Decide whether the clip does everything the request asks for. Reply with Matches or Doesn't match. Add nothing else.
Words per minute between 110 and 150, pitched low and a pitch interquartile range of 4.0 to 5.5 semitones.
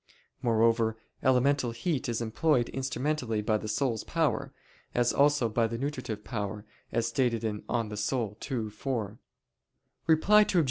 Doesn't match